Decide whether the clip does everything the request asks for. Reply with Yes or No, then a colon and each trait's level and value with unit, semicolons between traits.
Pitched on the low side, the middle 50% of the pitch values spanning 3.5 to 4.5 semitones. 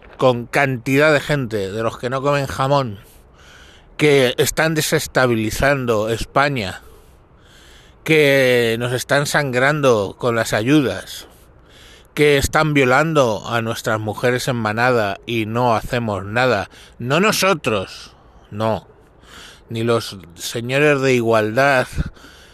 Yes: low, 125 Hz; average, 4.1 semitones